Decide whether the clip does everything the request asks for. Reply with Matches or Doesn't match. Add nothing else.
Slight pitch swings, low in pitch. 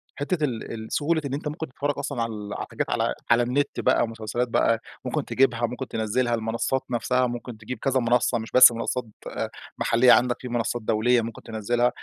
Matches